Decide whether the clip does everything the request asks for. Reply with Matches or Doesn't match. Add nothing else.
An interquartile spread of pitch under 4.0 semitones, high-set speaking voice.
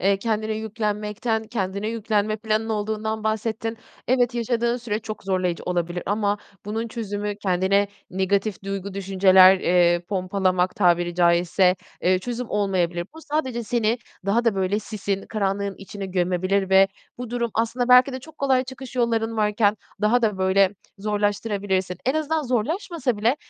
Matches